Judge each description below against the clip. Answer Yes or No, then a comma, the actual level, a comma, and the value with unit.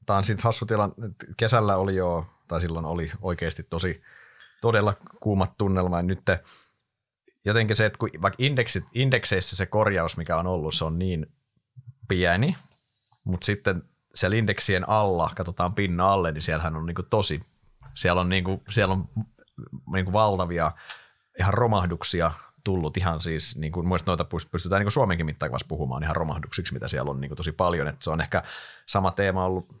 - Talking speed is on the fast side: Yes, fast, 170 wpm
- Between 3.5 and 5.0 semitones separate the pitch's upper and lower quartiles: Yes, average, 3.9 semitones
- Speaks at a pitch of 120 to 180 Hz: No, very low, 95 Hz